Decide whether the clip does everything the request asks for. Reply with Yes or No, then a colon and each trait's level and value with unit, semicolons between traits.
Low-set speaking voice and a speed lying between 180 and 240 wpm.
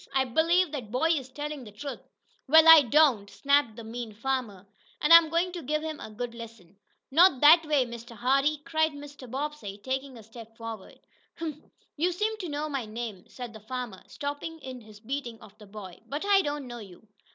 No: very high, 265 Hz; average, 200 wpm